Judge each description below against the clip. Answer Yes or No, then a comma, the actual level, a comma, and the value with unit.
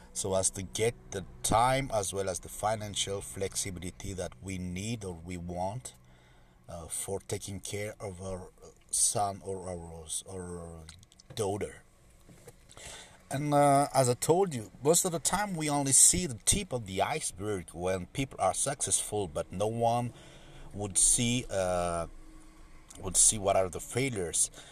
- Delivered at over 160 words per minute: No, average, 155 wpm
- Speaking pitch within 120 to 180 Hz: No, low, 100 Hz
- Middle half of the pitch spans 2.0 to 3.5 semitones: No, average, 4.9 semitones